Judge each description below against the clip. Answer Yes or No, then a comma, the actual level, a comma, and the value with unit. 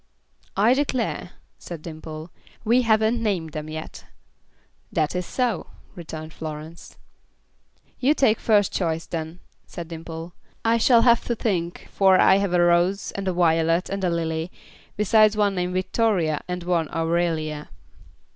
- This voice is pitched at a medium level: Yes, medium, 180 Hz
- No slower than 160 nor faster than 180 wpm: No, average, 145 wpm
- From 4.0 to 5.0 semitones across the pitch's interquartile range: Yes, average, 4.6 semitones